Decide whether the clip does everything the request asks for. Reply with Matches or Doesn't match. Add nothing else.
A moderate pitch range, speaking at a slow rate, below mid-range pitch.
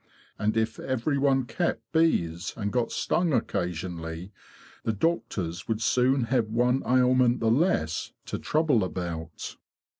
Doesn't match